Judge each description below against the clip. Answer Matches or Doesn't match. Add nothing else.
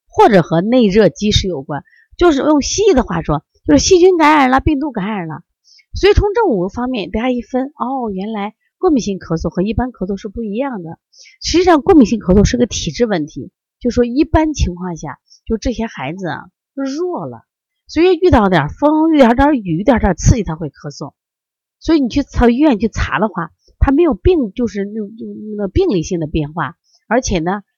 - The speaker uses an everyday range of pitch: Doesn't match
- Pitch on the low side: Doesn't match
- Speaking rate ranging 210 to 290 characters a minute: Doesn't match